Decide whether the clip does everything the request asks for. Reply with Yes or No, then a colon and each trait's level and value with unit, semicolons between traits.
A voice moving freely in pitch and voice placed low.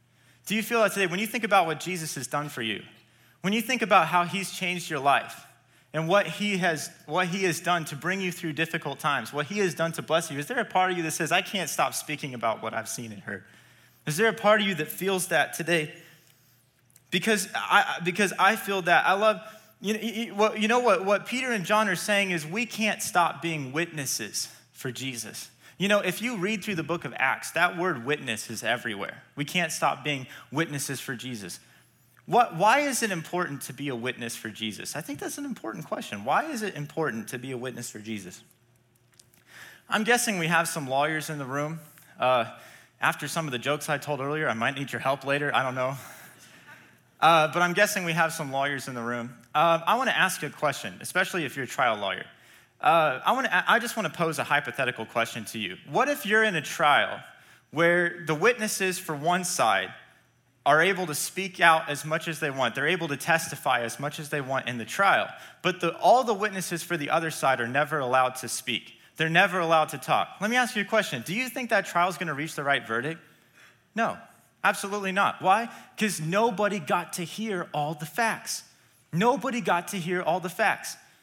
No: wide, 5.9 semitones; medium, 165 Hz